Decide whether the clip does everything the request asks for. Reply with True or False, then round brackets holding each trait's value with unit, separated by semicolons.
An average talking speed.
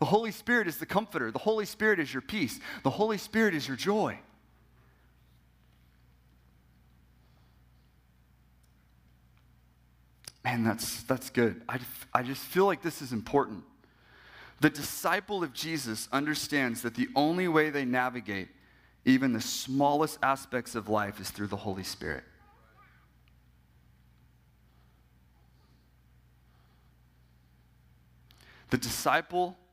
False (110 wpm)